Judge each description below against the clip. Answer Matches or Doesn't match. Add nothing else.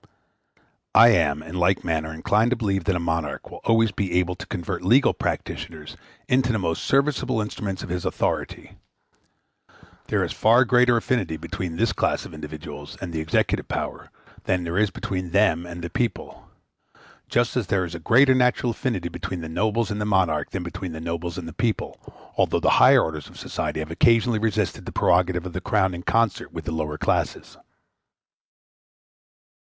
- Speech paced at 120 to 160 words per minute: Doesn't match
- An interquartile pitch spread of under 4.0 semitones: Doesn't match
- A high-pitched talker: Doesn't match